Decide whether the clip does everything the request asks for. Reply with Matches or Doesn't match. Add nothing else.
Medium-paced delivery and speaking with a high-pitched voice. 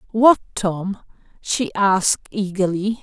Doesn't match